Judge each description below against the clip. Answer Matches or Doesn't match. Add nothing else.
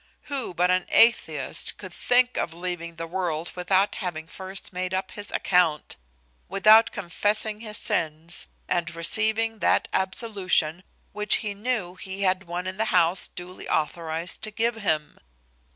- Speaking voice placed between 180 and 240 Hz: Matches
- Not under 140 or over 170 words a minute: Matches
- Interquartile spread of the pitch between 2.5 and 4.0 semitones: Matches